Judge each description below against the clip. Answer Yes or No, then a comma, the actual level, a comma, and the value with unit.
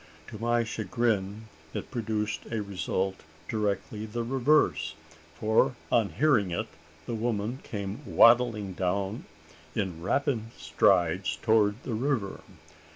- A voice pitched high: No, low, 110 Hz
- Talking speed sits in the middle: No, slow, 115 wpm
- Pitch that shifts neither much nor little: Yes, average, 3.0 semitones